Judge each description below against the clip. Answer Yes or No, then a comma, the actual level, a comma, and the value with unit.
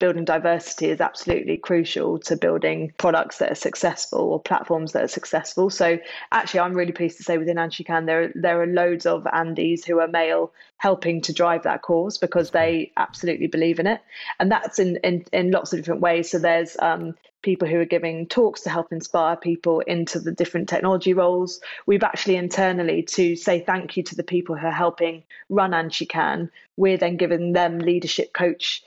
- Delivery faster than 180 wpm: Yes, average, 195 wpm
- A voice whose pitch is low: No, medium, 170 Hz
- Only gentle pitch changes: Yes, narrow, 1.3 semitones